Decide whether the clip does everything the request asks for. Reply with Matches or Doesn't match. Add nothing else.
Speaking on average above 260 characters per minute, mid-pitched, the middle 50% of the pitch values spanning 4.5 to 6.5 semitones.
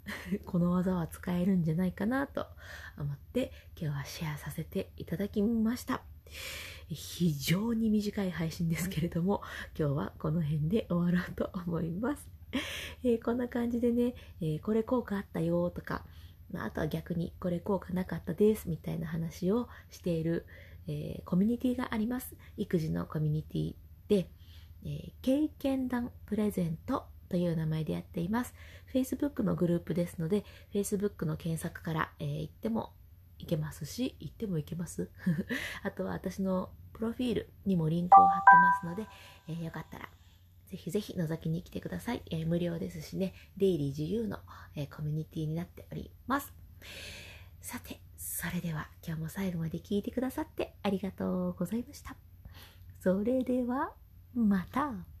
Matches